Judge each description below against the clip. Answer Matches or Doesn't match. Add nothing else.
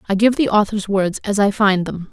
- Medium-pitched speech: Doesn't match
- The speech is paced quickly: Matches